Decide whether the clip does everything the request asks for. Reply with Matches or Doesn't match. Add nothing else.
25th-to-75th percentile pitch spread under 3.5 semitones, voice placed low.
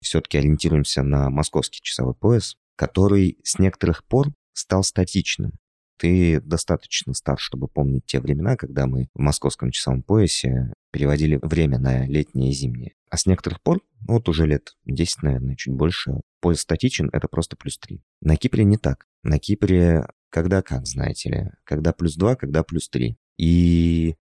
Doesn't match